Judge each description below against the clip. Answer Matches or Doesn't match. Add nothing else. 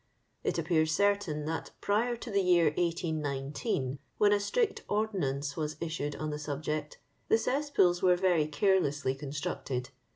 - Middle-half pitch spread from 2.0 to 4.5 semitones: Doesn't match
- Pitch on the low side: Doesn't match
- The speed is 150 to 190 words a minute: Doesn't match